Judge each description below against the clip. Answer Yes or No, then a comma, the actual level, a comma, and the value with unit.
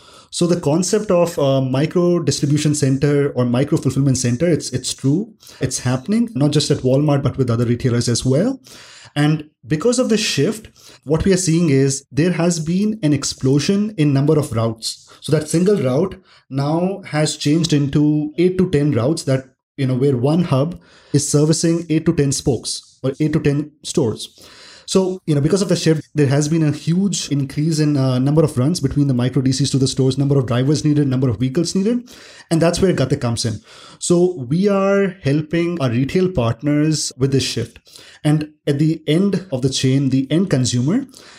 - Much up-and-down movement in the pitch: No, average, 4.0 semitones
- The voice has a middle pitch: Yes, medium, 150 Hz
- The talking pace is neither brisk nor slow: Yes, average, 195 wpm